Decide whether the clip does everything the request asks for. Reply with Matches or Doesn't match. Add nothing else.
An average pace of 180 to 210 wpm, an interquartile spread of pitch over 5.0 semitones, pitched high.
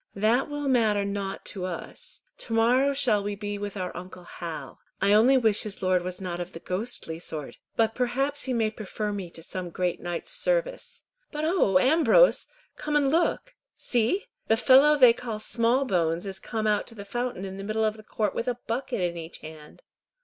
Matches